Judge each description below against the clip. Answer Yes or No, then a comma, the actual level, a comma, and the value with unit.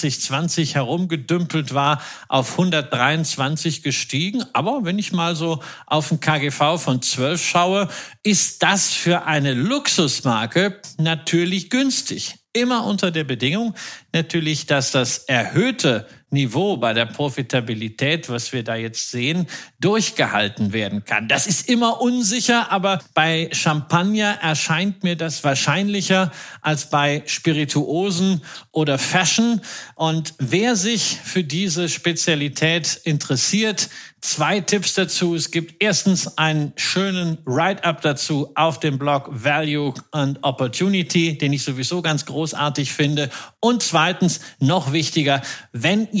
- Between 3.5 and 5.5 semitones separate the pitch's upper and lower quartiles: Yes, average, 4.4 semitones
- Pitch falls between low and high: Yes, medium, 160 Hz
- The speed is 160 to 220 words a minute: No, slow, 125 wpm